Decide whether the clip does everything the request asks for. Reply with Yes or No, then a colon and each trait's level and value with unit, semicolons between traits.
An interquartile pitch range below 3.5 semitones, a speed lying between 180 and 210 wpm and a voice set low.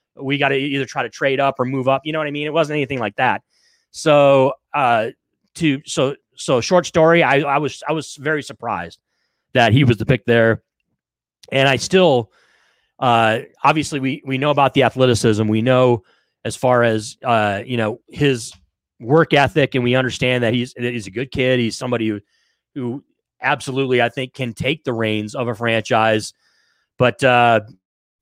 Yes: average, 3.1 semitones; average, 190 wpm; low, 130 Hz